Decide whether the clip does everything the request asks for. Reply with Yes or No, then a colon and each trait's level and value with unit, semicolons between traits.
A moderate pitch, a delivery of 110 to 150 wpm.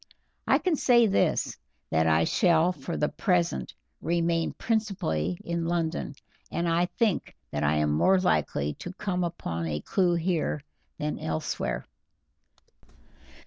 Yes: medium, 170 Hz; slow, 135 wpm